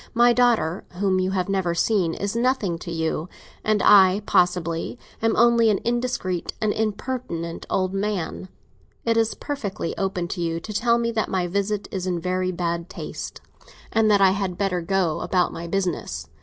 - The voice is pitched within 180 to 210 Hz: Yes, high, 190 Hz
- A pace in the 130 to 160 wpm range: No, average, 175 wpm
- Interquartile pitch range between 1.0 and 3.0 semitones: No, average, 3.6 semitones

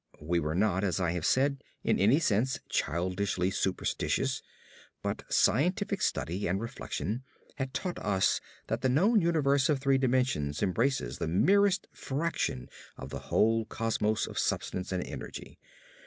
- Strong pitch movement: Yes, wide, 7.0 semitones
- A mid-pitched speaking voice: No, low, 115 Hz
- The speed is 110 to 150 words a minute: Yes, average, 145 wpm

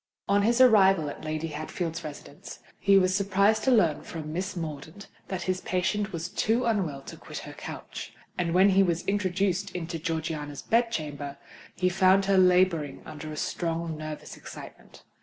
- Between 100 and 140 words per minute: No, average, 170 wpm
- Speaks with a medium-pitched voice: Yes, medium, 180 Hz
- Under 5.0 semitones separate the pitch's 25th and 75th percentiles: Yes, average, 4.0 semitones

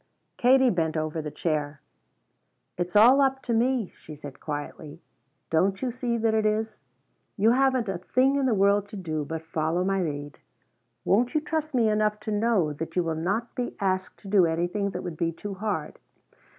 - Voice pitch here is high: Yes, high, 195 Hz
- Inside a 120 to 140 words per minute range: No, average, 190 wpm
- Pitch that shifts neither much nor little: No, wide, 6.1 semitones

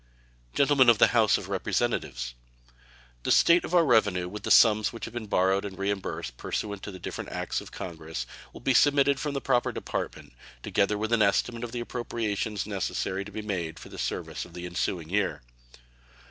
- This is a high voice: No, low, 105 Hz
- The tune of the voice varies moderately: Yes, average, 4.2 semitones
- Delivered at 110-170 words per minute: No, average, 190 wpm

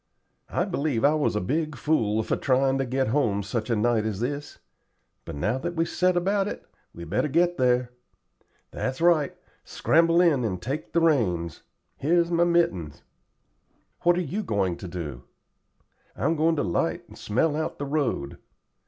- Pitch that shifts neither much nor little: No, wide, 7.5 semitones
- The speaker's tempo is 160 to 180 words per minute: Yes, average, 170 wpm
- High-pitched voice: No, low, 135 Hz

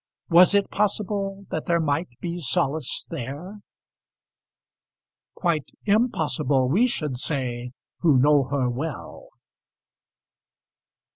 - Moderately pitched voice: Yes, medium, 160 Hz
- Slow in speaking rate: Yes, slow, 95 wpm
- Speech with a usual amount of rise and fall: No, wide, 5.9 semitones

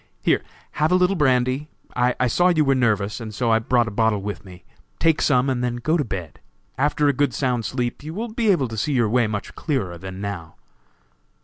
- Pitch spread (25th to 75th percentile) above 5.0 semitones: Yes, wide, 5.4 semitones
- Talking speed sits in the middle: No, fast, 215 wpm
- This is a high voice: No, low, 125 Hz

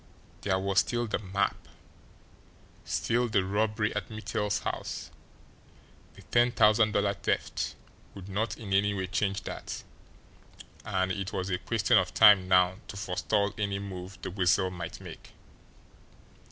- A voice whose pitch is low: Yes, low, 100 Hz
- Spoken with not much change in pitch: Yes, narrow, 2.0 semitones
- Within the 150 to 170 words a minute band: No, average, 140 wpm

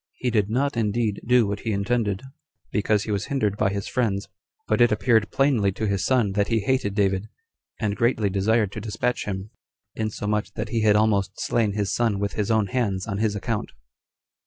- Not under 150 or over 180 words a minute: No, average, 195 wpm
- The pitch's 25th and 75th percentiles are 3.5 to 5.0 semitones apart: No, narrow, 2.4 semitones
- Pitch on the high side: No, low, 105 Hz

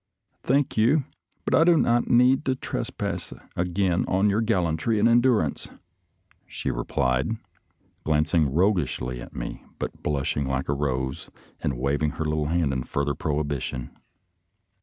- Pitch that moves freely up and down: Yes, wide, 8.0 semitones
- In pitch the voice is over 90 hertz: No, very low, 80 Hz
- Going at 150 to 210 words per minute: No, average, 140 wpm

